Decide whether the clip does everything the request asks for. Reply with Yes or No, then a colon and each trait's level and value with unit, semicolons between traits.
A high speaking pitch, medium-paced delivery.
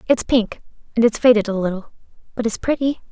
Yes: high, 230 Hz; average, 195 wpm